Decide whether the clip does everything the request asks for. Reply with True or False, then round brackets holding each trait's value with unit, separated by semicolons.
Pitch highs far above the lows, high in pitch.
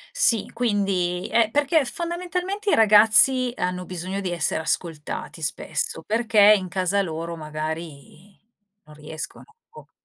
True (6.2 semitones; 200 Hz)